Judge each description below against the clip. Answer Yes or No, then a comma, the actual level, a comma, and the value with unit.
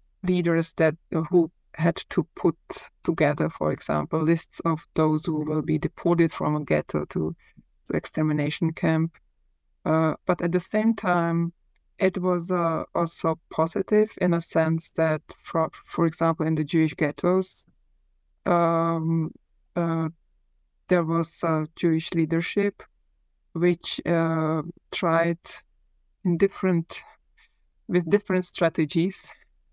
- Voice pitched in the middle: Yes, medium, 165 Hz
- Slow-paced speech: Yes, slow, 120 wpm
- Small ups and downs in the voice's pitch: Yes, narrow, 1.7 semitones